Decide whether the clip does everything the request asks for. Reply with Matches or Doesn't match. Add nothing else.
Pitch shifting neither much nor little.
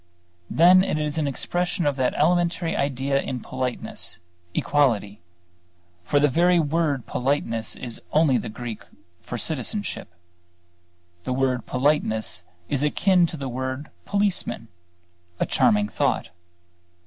Matches